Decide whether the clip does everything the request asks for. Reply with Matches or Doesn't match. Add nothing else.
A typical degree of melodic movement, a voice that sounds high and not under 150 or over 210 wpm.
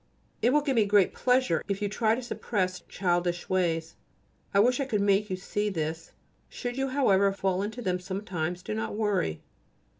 Matches